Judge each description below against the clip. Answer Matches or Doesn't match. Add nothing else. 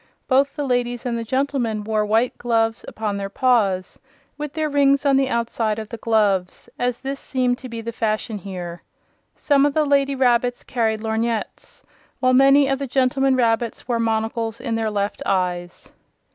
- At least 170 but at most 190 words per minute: Matches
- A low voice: Doesn't match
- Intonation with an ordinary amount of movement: Matches